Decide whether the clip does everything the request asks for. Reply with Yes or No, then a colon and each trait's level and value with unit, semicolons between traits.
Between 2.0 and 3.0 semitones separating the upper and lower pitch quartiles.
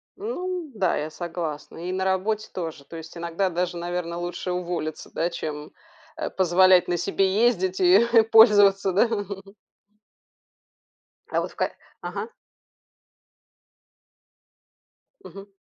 Yes: narrow, 2.5 semitones